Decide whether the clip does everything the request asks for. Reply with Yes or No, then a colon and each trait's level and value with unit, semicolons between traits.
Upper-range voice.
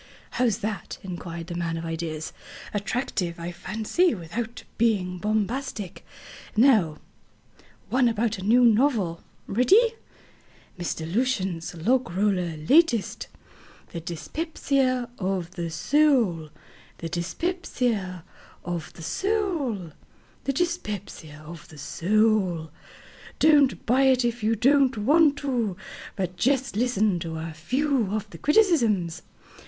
Yes: high, 215 Hz